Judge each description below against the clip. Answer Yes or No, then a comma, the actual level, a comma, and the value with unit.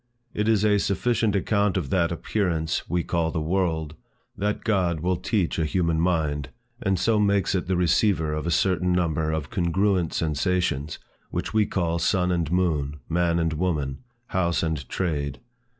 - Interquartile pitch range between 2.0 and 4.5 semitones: Yes, average, 3.1 semitones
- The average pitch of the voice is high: No, very low, 85 Hz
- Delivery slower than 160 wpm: No, average, 165 wpm